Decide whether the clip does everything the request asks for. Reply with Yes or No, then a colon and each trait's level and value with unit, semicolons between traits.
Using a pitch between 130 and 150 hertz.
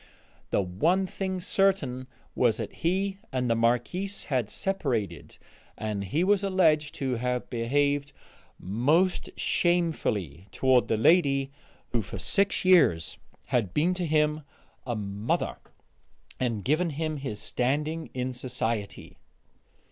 Yes: low, 135 Hz